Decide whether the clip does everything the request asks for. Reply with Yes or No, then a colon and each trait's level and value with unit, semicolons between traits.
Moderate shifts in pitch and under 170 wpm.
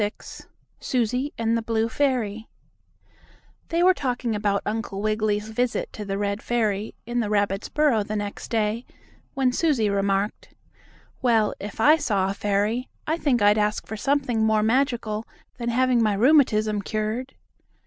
Yes: average, 3.1 semitones; average, 155 wpm